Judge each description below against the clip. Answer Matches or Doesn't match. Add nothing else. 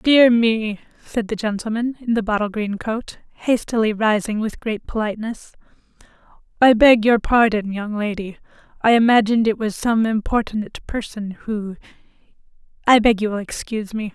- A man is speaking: Doesn't match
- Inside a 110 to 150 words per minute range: Matches